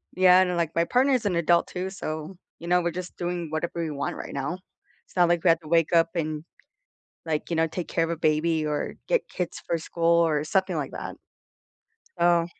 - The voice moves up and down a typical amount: No, narrow, 2.1 semitones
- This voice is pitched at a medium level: Yes, medium, 170 Hz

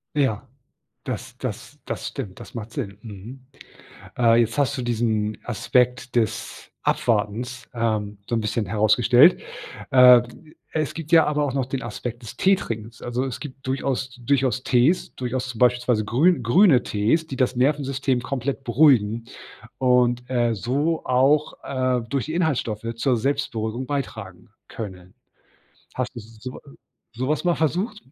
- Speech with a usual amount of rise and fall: Yes, average, 3.2 semitones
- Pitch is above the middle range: No, low, 125 Hz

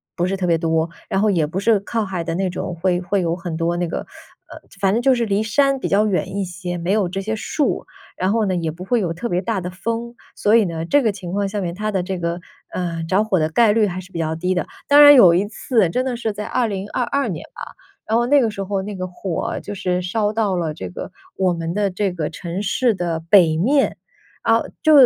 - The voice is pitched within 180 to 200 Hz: Yes, high, 190 Hz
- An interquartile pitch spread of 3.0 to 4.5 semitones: Yes, average, 3.7 semitones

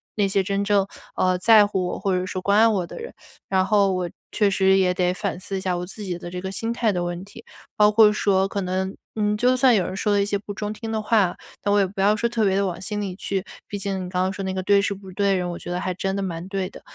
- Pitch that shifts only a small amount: Yes, narrow, 2.0 semitones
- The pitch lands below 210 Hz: Yes, high, 195 Hz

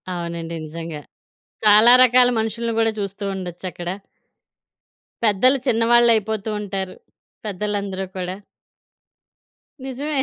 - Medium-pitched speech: No, high, 205 Hz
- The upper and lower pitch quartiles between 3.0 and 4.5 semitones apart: Yes, average, 3.9 semitones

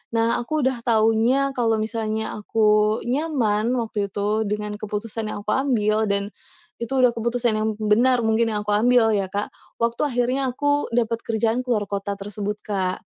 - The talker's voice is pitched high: Yes, high, 225 Hz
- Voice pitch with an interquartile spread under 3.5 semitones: Yes, narrow, 2.5 semitones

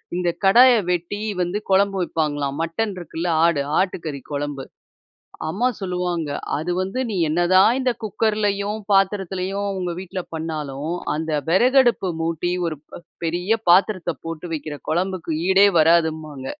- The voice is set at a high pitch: No, medium, 180 Hz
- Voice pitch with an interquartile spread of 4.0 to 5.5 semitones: No, average, 3.6 semitones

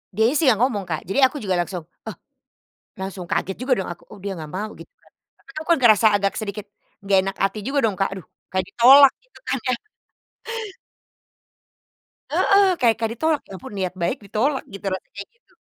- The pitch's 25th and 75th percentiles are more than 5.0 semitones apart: Yes, wide, 5.4 semitones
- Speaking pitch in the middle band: No, high, 210 Hz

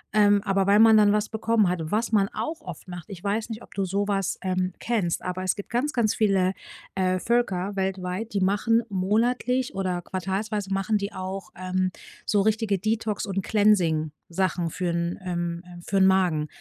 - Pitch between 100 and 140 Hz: No, high, 195 Hz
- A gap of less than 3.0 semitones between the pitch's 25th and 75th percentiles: Yes, narrow, 2.6 semitones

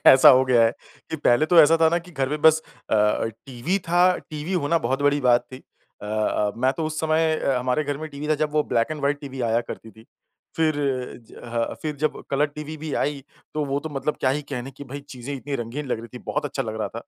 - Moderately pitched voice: Yes, medium, 145 Hz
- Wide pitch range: No, average, 3.3 semitones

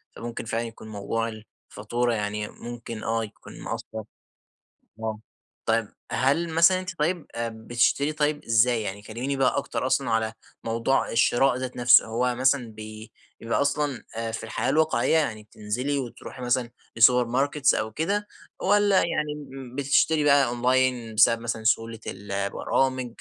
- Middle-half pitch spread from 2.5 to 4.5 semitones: Yes, average, 3.9 semitones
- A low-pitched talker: Yes, low, 120 Hz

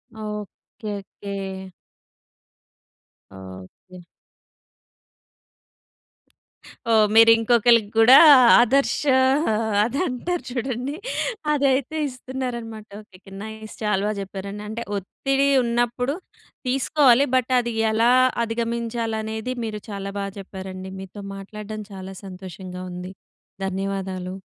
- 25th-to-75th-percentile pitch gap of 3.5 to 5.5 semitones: Yes, average, 3.8 semitones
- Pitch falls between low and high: No, high, 220 Hz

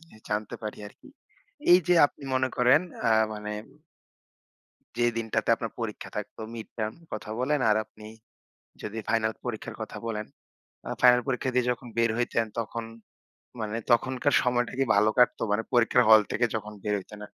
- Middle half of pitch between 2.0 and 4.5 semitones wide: Yes, narrow, 2.5 semitones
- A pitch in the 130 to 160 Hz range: No, low, 115 Hz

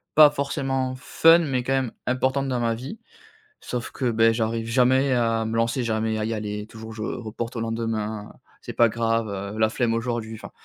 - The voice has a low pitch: Yes, low, 115 Hz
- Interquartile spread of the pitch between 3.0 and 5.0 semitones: No, narrow, 2.5 semitones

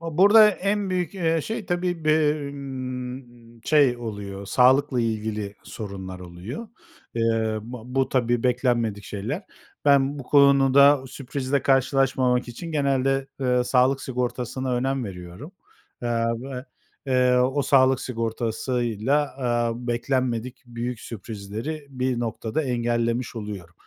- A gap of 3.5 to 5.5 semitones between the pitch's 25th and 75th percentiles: No, average, 3.1 semitones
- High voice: No, low, 125 Hz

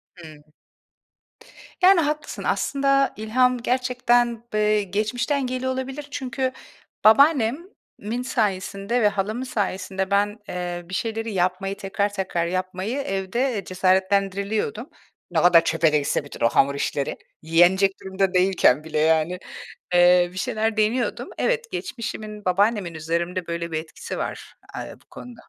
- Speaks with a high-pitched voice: Yes, high, 200 Hz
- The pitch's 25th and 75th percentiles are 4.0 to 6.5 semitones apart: Yes, average, 5.1 semitones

